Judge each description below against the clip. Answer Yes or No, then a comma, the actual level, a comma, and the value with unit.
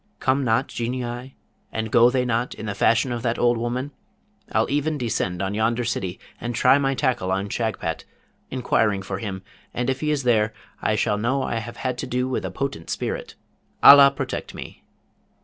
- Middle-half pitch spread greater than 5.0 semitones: No, average, 2.9 semitones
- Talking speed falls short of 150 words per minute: No, average, 190 wpm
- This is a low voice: Yes, low, 120 Hz